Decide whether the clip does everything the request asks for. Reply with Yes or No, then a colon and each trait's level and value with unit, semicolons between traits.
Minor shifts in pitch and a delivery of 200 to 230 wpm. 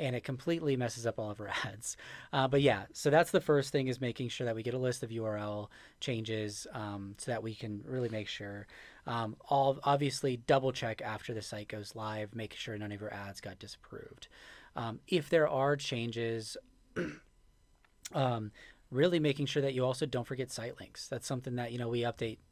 No: average, 3.9 semitones; fast, 205 wpm